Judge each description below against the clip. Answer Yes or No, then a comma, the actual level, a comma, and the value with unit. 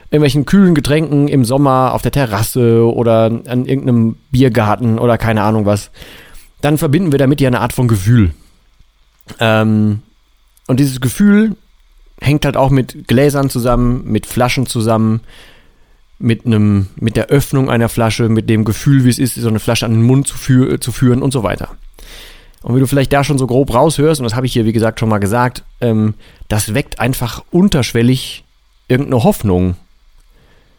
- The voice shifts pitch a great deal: No, average, 3.5 semitones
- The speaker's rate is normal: Yes, average, 175 wpm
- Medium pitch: No, low, 125 Hz